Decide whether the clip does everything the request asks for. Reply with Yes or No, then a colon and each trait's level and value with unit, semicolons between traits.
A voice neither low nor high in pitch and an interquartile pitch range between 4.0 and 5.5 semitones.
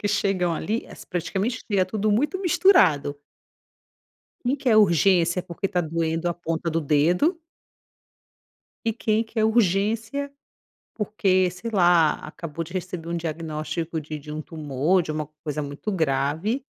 Yes: medium, 180 Hz; average, 5.0 semitones